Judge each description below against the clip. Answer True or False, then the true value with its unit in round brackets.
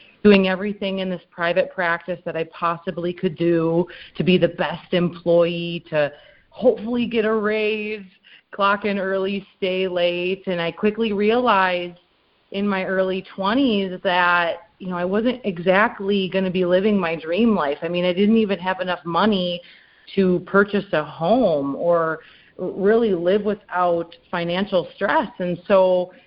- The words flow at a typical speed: True (155 wpm)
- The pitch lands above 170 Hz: True (185 Hz)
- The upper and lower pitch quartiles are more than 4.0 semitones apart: False (2.7 semitones)